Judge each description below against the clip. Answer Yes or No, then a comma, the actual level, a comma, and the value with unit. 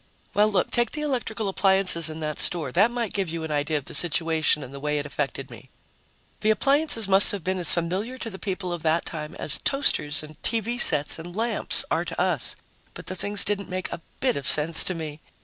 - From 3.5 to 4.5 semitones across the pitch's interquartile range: No, average, 5.2 semitones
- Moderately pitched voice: Yes, medium, 180 Hz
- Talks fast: Yes, fast, 225 wpm